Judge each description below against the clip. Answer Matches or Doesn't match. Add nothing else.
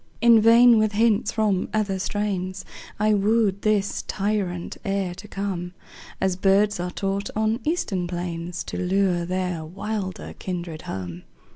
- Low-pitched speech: Doesn't match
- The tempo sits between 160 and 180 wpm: Doesn't match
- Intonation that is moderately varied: Matches